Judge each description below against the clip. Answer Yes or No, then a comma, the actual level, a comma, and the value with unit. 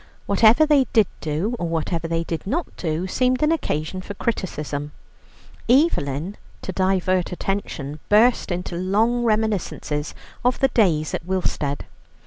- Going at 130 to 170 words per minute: Yes, slow, 135 wpm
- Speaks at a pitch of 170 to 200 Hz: Yes, medium, 185 Hz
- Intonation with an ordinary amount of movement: No, wide, 5.9 semitones